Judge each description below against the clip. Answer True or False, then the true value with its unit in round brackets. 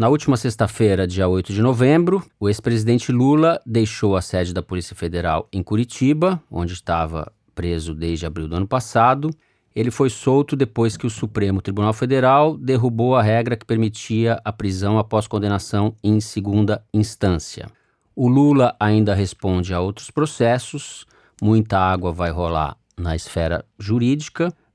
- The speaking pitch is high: False (110 Hz)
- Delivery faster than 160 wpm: False (150 wpm)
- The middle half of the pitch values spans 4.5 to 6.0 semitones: True (5.0 semitones)